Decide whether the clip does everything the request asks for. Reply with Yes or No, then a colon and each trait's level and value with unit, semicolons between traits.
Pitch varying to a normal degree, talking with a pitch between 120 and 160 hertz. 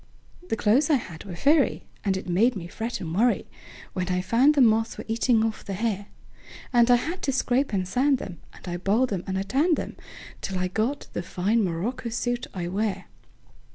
No: average, 4.9 semitones; high, 220 Hz